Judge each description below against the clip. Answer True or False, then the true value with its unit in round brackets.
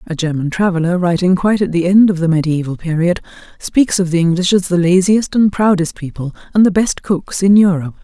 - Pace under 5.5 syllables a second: False (5.7 syllables/s)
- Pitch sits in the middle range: True (180 Hz)